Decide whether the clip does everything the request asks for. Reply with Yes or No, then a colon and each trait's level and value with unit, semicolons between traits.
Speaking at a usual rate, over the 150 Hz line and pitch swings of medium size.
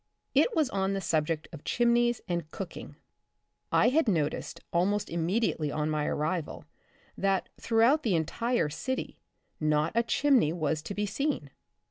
No: average, 145 wpm; high, 190 Hz; wide, 7.2 semitones